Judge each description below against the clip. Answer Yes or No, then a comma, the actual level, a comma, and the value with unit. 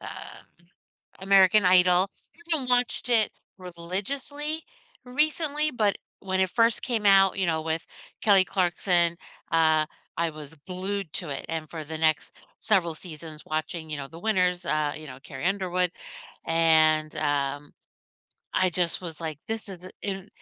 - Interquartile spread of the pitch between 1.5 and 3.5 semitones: No, average, 4.0 semitones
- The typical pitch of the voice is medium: Yes, medium, 180 Hz